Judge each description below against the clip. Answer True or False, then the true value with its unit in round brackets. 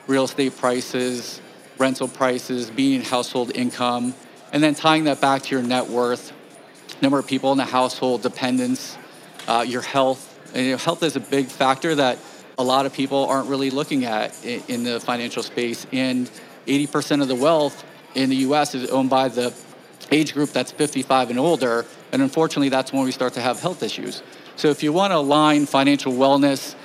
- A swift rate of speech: False (185 wpm)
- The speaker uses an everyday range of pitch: False (2.0 semitones)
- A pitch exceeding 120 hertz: True (135 Hz)